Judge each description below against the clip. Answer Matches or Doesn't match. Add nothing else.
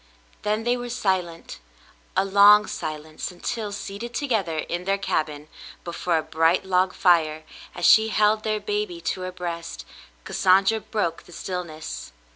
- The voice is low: Doesn't match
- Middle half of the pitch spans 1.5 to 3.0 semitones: Doesn't match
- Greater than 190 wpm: Doesn't match